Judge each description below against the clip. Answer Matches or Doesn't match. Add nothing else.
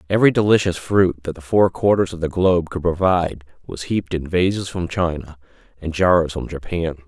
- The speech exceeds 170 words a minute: Matches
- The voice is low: Matches